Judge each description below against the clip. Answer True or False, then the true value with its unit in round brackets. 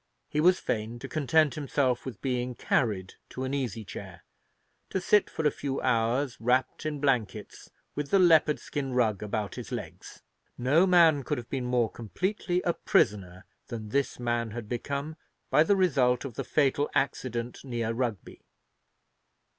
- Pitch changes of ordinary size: True (4.0 semitones)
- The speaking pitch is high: False (130 Hz)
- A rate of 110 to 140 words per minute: False (160 wpm)